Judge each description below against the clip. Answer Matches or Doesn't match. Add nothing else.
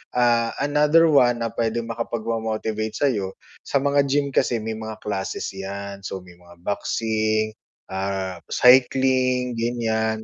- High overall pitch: Doesn't match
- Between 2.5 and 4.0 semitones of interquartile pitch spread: Matches